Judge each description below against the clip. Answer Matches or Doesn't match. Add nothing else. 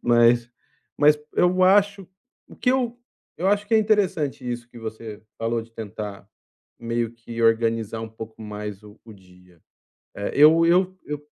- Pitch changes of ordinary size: Doesn't match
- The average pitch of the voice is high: Doesn't match